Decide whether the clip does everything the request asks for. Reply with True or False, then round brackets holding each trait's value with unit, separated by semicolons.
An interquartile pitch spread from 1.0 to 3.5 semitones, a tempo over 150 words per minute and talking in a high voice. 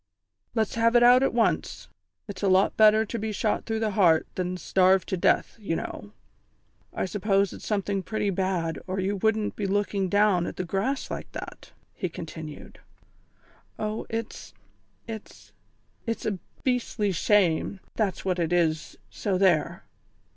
True (3.0 semitones; 160 wpm; 200 Hz)